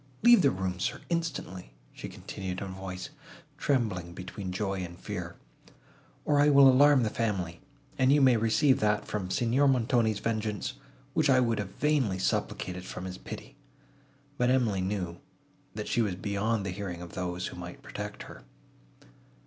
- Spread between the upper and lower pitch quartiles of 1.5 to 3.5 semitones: No, wide, 5.6 semitones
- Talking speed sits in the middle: Yes, average, 165 wpm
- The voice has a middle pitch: No, low, 105 Hz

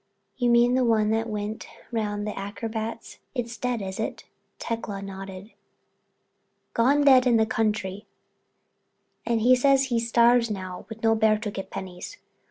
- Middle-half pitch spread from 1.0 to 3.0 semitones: Yes, narrow, 2.5 semitones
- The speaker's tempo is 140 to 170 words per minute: Yes, average, 160 wpm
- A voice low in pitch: No, high, 225 Hz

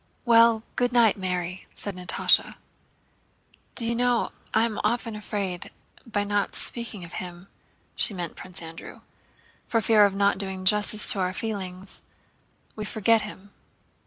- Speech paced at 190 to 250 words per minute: No, average, 150 wpm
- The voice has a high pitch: Yes, high, 205 Hz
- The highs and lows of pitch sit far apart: No, average, 3.4 semitones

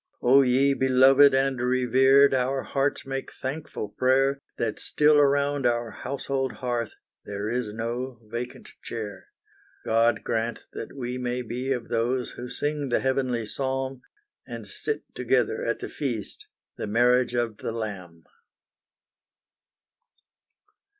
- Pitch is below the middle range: Yes, low, 125 Hz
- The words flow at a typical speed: No, slow, 130 wpm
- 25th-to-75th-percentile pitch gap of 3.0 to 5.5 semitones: No, narrow, 2.4 semitones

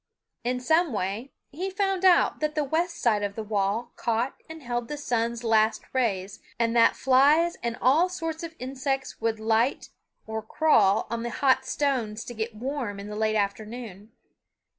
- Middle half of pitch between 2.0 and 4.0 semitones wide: No, average, 4.7 semitones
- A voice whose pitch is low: No, high, 240 Hz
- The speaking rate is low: No, average, 175 wpm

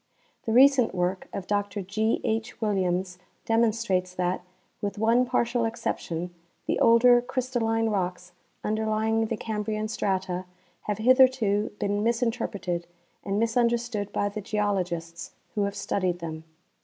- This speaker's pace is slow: Yes, slow, 130 wpm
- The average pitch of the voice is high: Yes, high, 210 Hz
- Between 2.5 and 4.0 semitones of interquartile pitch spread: Yes, average, 3.5 semitones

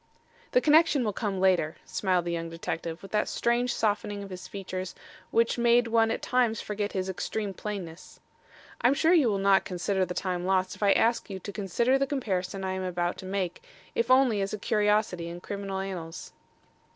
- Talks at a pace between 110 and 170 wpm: No, average, 195 wpm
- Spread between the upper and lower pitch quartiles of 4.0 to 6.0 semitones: No, average, 3.5 semitones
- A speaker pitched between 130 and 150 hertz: No, high, 195 Hz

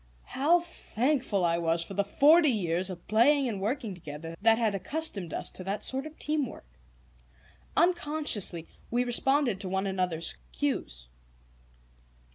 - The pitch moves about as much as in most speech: No, wide, 7.8 semitones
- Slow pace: No, average, 145 wpm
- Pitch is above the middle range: Yes, high, 215 Hz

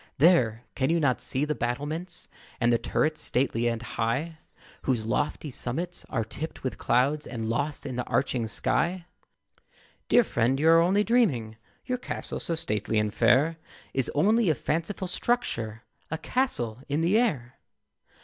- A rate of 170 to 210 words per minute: No, average, 160 wpm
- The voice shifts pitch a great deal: Yes, wide, 5.8 semitones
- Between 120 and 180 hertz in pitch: Yes, medium, 140 Hz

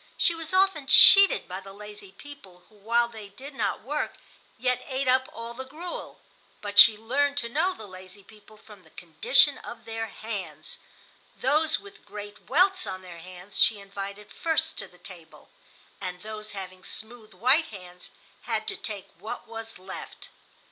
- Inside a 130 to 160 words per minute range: No, average, 170 wpm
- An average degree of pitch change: No, wide, 5.9 semitones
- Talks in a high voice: Yes, high, 220 Hz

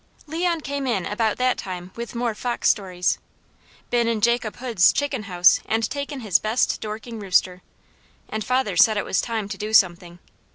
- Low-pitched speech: No, high, 220 Hz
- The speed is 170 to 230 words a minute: Yes, average, 175 wpm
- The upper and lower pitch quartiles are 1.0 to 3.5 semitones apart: No, average, 4.1 semitones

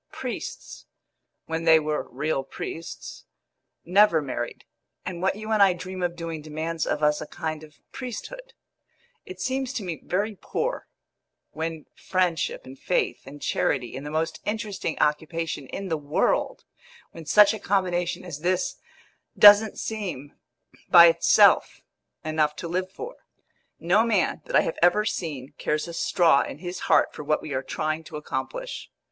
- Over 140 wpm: Yes, average, 160 wpm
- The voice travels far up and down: No, average, 4.4 semitones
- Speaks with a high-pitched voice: No, medium, 165 Hz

